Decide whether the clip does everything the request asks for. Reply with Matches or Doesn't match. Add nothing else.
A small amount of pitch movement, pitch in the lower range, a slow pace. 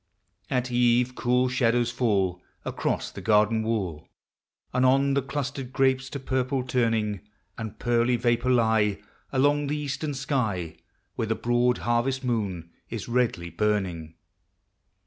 Doesn't match